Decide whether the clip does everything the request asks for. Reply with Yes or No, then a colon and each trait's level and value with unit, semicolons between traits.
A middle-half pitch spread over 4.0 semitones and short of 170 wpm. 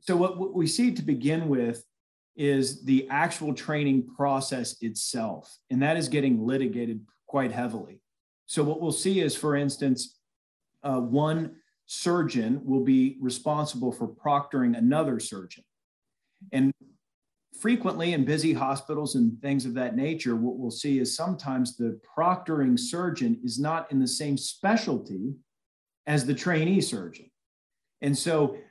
Yes: average, 4.8 semitones; average, 140 wpm